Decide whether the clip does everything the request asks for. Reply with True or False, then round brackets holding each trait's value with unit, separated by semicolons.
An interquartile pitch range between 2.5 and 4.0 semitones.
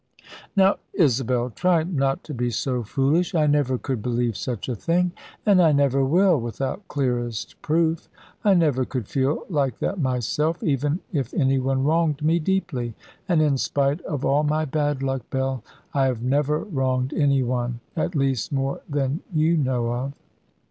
True (3.5 semitones)